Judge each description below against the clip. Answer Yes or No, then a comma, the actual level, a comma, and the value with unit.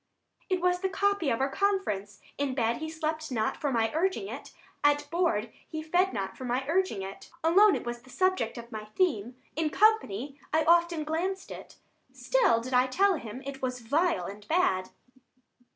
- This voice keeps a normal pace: Yes, average, 195 wpm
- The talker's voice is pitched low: No, very high, 295 Hz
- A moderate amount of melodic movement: No, wide, 7.2 semitones